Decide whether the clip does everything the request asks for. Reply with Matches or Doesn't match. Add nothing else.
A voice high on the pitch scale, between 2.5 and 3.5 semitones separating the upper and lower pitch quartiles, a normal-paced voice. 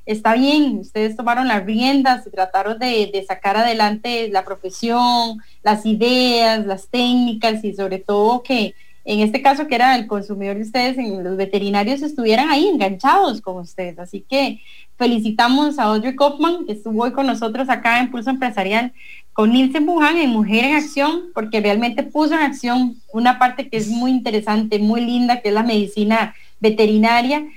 Matches